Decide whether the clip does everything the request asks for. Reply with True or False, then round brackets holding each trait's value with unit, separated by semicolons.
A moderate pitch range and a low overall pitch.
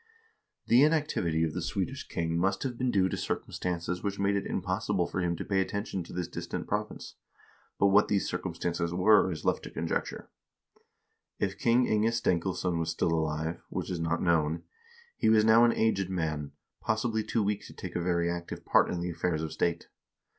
True (3.8 semitones; 90 Hz)